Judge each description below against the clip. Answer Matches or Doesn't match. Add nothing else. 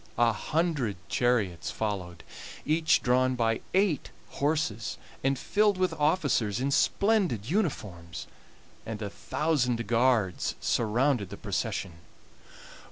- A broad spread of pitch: Matches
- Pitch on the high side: Doesn't match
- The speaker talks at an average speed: Doesn't match